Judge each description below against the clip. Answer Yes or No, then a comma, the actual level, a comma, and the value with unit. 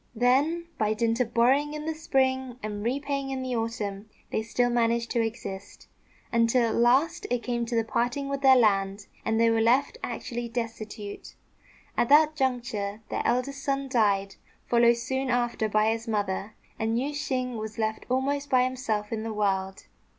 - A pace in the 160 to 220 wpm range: Yes, average, 170 wpm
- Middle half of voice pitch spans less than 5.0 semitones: Yes, average, 3.2 semitones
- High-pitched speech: Yes, high, 235 Hz